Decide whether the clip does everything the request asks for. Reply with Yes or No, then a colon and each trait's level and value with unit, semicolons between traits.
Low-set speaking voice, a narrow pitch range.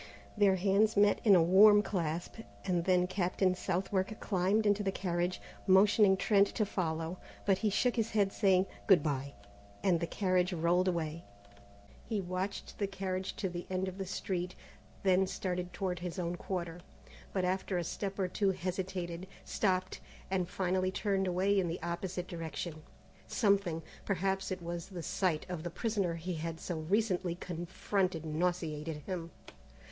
No: medium, 185 Hz; narrow, 2.1 semitones